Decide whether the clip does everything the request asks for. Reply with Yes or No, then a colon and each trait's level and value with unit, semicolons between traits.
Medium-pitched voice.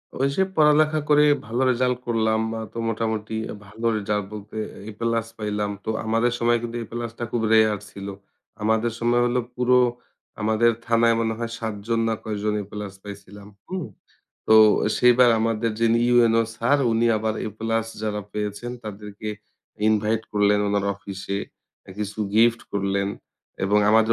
No: low, 110 Hz